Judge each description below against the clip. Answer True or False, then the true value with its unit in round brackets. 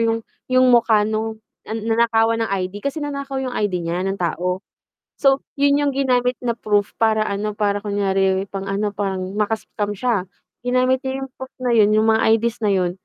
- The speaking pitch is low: False (220 Hz)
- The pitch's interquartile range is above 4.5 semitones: False (3.8 semitones)